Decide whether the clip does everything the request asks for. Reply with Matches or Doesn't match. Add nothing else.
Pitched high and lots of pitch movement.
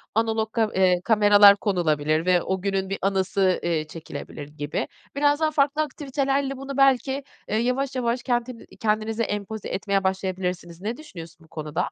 Matches